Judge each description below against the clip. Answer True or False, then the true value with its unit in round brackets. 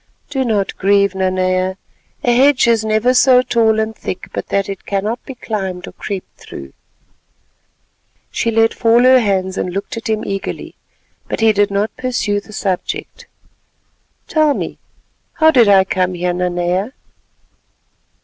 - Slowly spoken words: False (150 wpm)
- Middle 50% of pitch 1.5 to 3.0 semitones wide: False (3.8 semitones)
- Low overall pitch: False (205 Hz)